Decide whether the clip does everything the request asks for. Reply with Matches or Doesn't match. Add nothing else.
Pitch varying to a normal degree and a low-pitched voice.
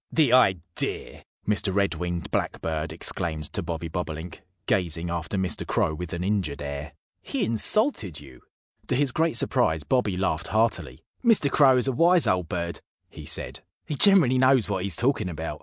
Doesn't match